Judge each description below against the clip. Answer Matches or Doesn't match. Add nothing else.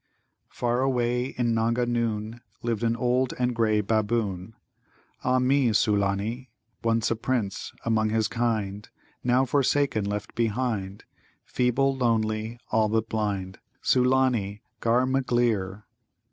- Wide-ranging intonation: Doesn't match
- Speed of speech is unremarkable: Doesn't match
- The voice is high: Doesn't match